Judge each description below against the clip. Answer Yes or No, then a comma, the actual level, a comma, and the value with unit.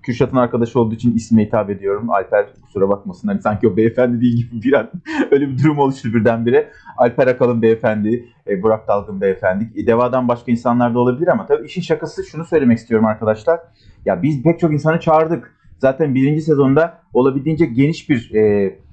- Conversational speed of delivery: No, fast, 175 wpm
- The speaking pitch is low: Yes, low, 125 Hz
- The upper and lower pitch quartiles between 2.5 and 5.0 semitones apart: No, wide, 5.6 semitones